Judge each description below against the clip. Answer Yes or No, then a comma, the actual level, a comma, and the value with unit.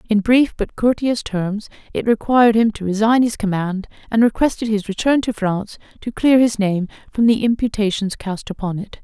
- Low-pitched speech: No, high, 215 Hz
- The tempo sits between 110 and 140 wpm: No, average, 185 wpm